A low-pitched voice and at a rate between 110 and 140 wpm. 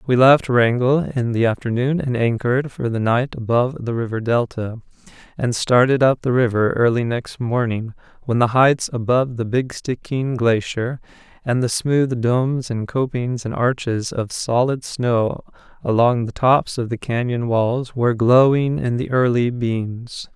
No: low, 120 Hz; average, 160 wpm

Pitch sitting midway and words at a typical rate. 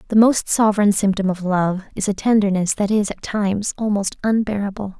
No: high, 205 Hz; average, 180 wpm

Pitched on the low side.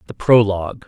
Yes: low, 105 Hz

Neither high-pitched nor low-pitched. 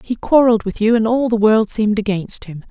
No: high, 215 Hz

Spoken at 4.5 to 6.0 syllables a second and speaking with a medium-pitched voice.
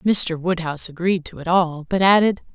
Yes: 5.0 syllables/s; medium, 175 Hz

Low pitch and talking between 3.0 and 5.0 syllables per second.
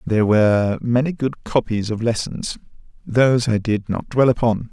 Yes: low, 115 Hz; 4.8 syllables/s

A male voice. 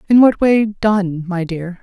No: female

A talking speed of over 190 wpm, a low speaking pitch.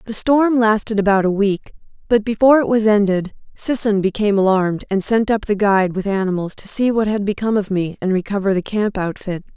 No: fast, 205 wpm; high, 205 Hz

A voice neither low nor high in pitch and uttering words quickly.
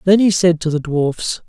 Yes: medium, 170 Hz; fast, 245 wpm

